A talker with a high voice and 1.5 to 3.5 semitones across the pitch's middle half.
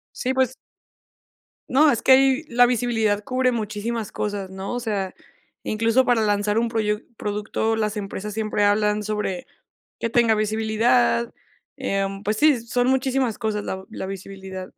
Yes: high, 220 Hz; average, 2.9 semitones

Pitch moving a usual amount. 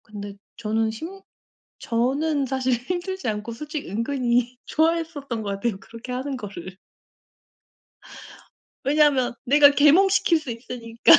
Yes: average, 4.7 semitones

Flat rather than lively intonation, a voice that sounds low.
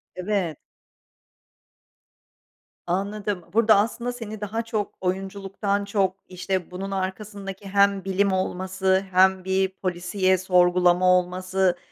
No: narrow, 1.6 semitones; high, 190 Hz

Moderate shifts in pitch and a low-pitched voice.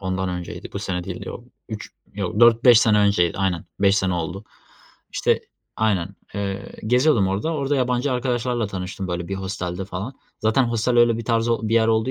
Yes: average, 3.9 semitones; low, 105 Hz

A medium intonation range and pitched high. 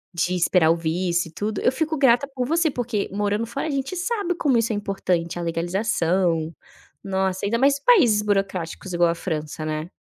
No: wide, 6.5 semitones; high, 195 Hz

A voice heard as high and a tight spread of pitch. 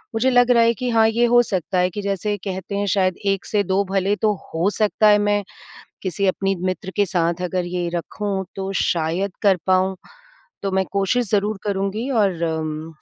Yes: high, 195 Hz; narrow, 2.3 semitones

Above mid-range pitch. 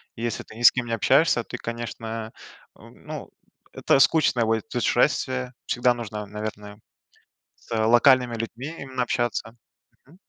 No: low, 115 Hz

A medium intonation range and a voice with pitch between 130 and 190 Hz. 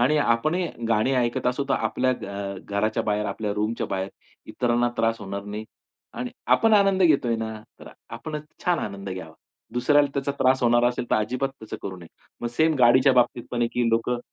No: average, 3.7 semitones; low, 120 Hz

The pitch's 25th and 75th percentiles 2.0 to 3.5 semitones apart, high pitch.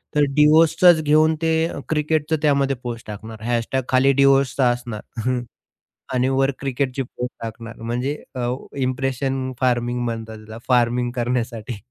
No: narrow, 2.6 semitones; low, 130 Hz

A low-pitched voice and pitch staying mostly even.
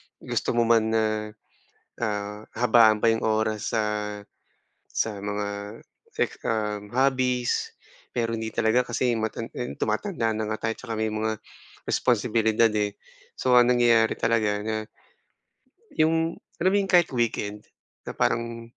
Yes: low, 115 Hz; narrow, 2.0 semitones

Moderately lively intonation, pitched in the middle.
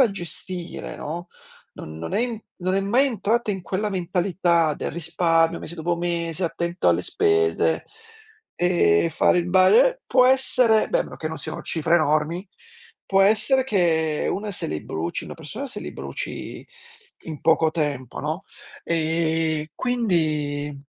Yes: average, 4.5 semitones; medium, 175 Hz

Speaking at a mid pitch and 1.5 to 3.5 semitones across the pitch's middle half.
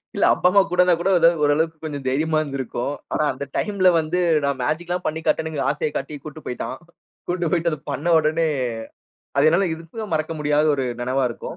Yes: medium, 155 Hz; average, 3.0 semitones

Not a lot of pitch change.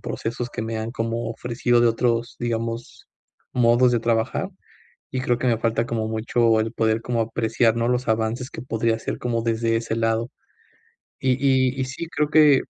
Yes: narrow, 1.4 semitones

